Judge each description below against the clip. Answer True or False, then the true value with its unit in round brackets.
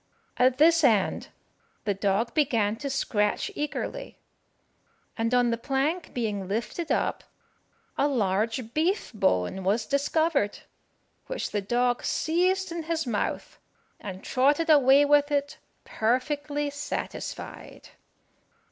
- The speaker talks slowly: True (115 wpm)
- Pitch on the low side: False (260 Hz)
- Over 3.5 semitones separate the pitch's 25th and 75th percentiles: True (5.4 semitones)